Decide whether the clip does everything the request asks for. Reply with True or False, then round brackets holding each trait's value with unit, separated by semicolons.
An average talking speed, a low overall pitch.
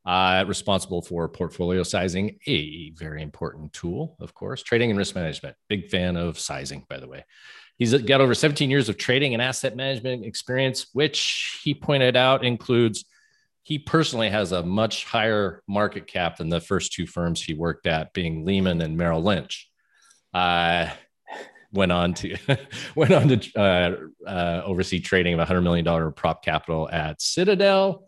True (165 wpm; 100 Hz)